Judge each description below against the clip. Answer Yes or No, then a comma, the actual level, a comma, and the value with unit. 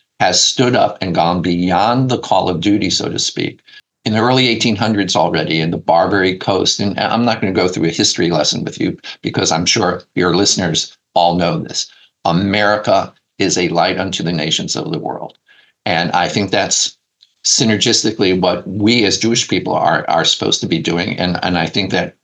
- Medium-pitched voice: No, low, 100 Hz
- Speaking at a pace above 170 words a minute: Yes, average, 195 wpm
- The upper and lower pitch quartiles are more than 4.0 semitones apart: Yes, average, 4.5 semitones